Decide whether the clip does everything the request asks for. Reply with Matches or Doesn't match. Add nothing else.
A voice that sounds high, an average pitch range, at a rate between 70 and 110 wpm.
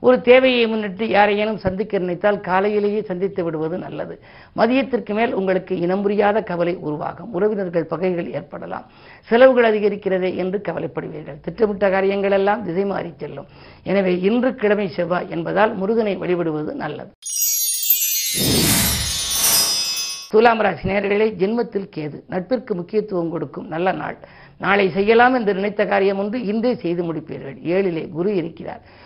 Doesn't match